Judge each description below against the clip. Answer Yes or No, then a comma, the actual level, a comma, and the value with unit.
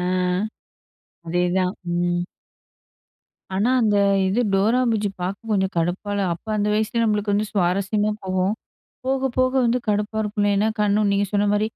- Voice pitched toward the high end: Yes, high, 205 Hz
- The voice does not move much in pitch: Yes, narrow, 2.2 semitones